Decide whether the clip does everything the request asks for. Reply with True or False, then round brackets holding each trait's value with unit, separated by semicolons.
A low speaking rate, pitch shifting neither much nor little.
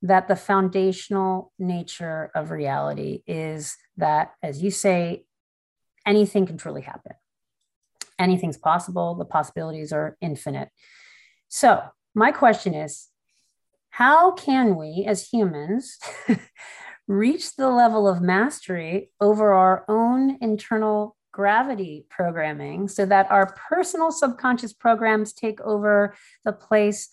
True (115 wpm; 4.2 semitones)